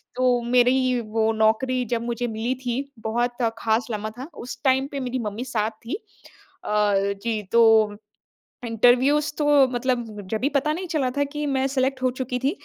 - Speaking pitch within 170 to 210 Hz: No, high, 245 Hz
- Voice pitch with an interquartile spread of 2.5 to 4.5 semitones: Yes, average, 2.9 semitones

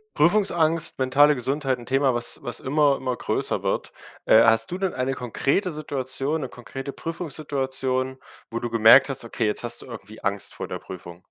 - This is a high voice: No, low, 130 Hz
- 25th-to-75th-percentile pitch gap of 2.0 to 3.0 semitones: No, average, 3.5 semitones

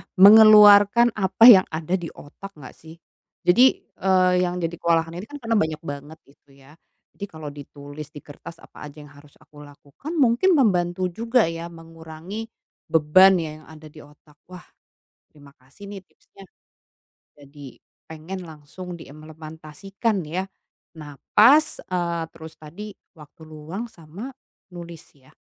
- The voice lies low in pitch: No, medium, 165 Hz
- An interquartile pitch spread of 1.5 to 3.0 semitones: No, average, 4.4 semitones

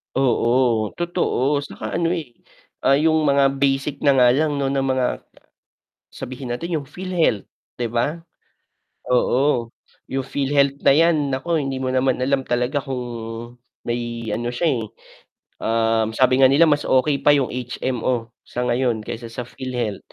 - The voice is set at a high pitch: No, low, 130 Hz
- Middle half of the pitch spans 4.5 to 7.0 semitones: No, average, 2.8 semitones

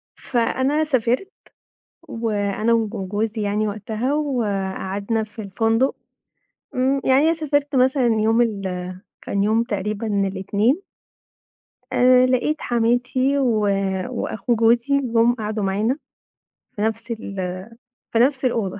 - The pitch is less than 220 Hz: No, high, 230 Hz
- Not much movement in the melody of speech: No, average, 3.7 semitones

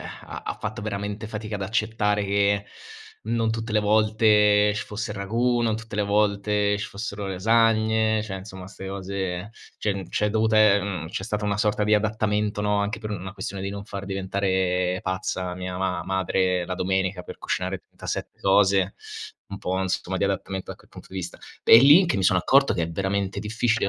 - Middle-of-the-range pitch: No, low, 100 Hz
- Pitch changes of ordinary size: No, narrow, 2.1 semitones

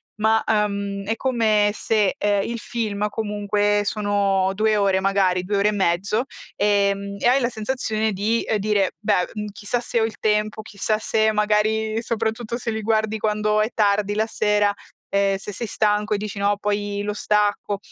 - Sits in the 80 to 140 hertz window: No, high, 210 Hz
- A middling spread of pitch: No, narrow, 1.3 semitones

